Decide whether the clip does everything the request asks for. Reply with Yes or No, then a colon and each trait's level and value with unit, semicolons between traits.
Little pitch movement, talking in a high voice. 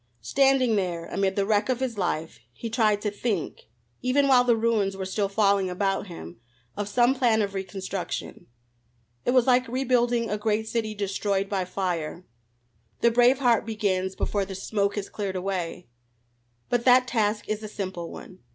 No: average, 3.6 semitones; high, 205 Hz